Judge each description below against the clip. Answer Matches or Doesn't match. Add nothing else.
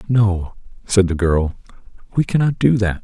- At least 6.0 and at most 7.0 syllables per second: Doesn't match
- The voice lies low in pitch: Matches